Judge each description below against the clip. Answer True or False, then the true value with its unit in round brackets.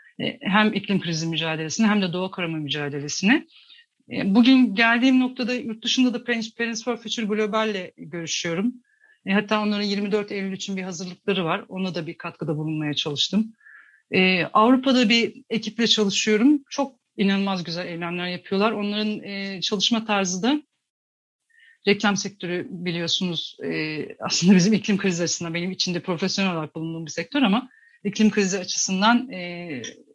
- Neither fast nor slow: True (130 wpm)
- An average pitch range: True (4.5 semitones)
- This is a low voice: False (200 Hz)